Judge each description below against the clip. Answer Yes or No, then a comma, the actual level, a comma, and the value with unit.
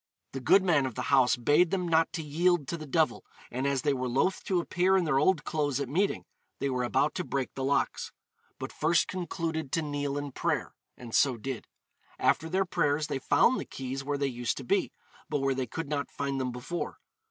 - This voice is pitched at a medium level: Yes, medium, 145 Hz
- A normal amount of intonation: Yes, average, 3.7 semitones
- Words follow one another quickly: Yes, fast, 220 wpm